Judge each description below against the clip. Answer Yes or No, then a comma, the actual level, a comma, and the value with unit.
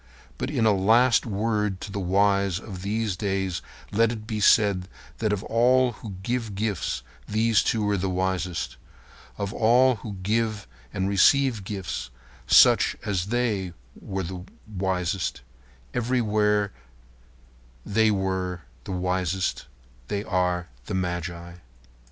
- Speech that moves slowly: Yes, slow, 125 wpm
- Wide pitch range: No, average, 3.0 semitones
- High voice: No, low, 100 Hz